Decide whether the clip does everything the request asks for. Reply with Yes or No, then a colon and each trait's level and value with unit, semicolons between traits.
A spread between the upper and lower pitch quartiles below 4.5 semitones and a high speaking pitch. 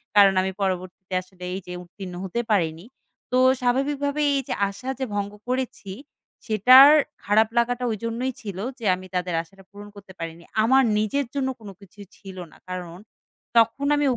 No: average, 5.1 semitones; high, 205 Hz